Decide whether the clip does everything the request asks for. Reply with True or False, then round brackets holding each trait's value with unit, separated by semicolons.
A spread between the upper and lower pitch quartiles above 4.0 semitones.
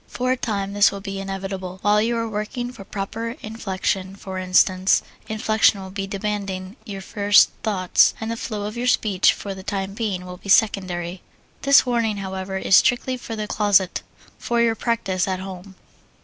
False (2.7 semitones)